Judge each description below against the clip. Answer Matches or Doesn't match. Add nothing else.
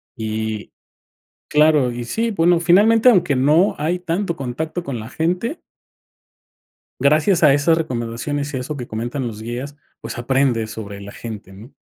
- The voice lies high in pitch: Doesn't match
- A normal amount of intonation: Doesn't match